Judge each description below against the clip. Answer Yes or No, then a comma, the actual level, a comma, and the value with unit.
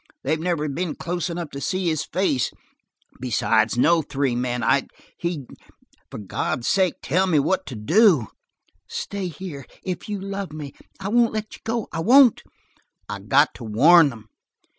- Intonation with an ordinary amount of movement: No, wide, 5.9 semitones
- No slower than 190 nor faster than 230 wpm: No, average, 165 wpm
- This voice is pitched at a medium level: Yes, medium, 165 Hz